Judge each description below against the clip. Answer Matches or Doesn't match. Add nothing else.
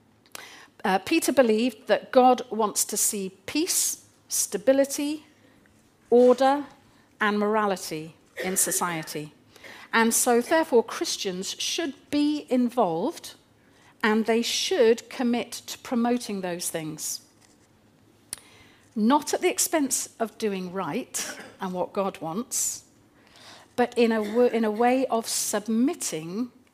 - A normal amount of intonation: Matches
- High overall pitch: Matches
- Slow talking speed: Matches